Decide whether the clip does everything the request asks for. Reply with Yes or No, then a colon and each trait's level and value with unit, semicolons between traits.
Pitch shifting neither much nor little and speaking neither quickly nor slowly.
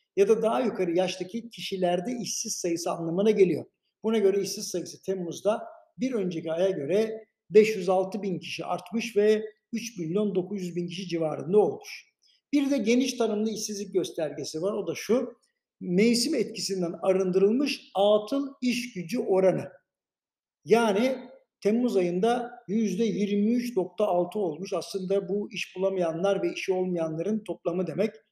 Yes: average, 3.7 semitones; average, 130 wpm